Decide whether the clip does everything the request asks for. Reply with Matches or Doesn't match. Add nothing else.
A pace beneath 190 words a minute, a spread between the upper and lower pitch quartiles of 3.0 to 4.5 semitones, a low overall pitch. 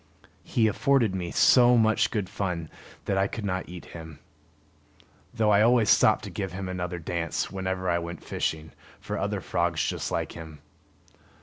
Matches